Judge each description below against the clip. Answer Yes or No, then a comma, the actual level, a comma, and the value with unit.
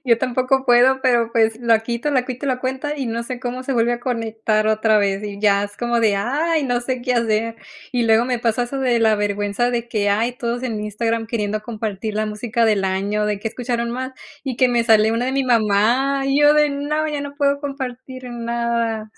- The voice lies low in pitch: No, high, 235 Hz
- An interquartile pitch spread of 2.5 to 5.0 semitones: Yes, average, 2.9 semitones